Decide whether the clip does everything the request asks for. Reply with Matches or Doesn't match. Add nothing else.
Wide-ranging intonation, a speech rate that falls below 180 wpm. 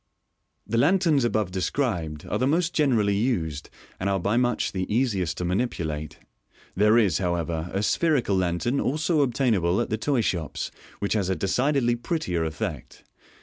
Matches